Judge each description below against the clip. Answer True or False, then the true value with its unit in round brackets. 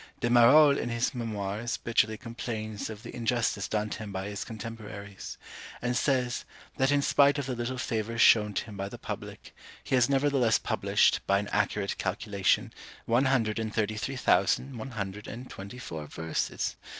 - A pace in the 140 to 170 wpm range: False (180 wpm)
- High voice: False (115 Hz)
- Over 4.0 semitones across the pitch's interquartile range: False (3.2 semitones)